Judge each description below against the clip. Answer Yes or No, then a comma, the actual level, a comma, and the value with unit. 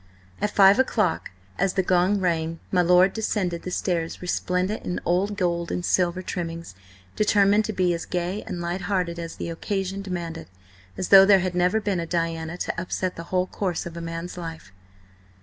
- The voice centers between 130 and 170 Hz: No, medium, 180 Hz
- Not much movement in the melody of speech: Yes, narrow, 2.2 semitones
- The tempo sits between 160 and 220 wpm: Yes, average, 185 wpm